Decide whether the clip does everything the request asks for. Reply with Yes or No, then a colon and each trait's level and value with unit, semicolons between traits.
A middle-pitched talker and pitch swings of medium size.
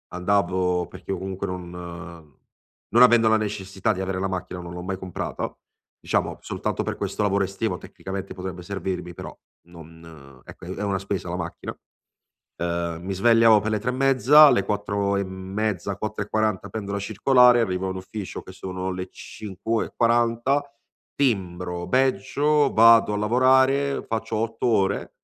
No: low, 100 Hz; average, 3.6 semitones